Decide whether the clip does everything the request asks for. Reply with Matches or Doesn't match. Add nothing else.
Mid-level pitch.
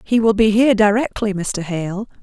Doesn't match